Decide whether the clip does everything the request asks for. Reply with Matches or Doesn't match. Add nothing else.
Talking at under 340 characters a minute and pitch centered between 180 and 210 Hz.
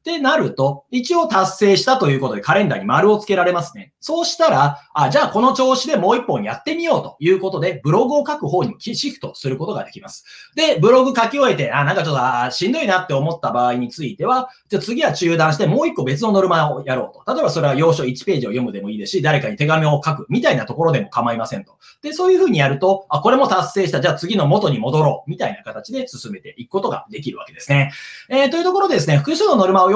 Doesn't match